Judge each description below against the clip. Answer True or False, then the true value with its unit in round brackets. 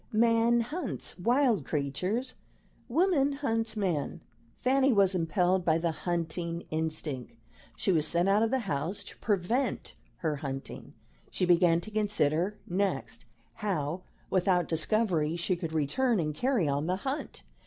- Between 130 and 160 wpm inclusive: True (140 wpm)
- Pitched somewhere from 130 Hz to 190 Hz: True (185 Hz)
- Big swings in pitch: True (6.0 semitones)